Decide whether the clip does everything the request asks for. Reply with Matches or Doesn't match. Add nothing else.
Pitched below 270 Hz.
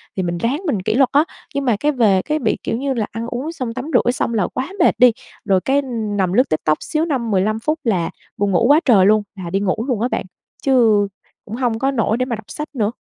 Matches